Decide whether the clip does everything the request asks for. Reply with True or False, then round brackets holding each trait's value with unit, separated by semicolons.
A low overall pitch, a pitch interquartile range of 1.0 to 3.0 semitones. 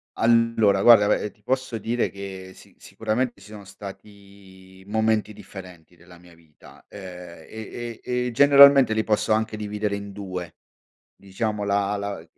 True (105 Hz; 2.7 semitones)